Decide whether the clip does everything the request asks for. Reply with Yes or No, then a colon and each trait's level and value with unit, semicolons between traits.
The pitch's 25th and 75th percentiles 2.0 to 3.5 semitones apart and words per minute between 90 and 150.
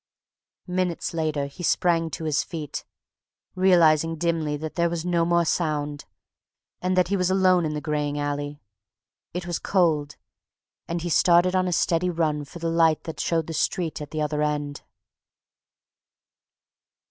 No: narrow, 2.6 semitones; average, 160 wpm